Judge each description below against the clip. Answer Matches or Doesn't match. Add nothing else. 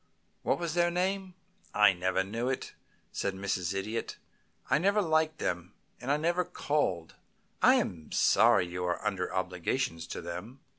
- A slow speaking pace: Doesn't match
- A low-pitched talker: Matches